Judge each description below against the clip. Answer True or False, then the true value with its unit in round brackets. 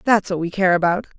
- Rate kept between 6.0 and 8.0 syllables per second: True (6.3 syllables/s)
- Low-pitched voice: False (190 Hz)